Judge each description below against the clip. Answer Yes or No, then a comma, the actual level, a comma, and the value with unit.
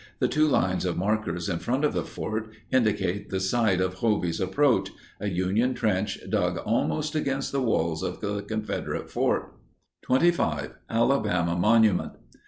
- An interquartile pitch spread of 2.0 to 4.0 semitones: No, average, 4.8 semitones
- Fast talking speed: No, average, 145 wpm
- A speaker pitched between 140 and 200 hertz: No, low, 105 Hz